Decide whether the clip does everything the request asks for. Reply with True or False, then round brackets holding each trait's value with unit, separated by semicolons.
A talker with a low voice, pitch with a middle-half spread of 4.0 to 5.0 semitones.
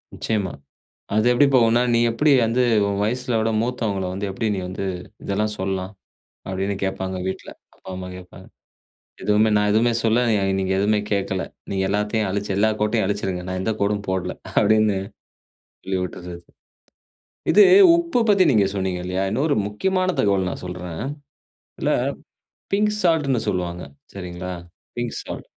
False (105 Hz; 3.3 semitones)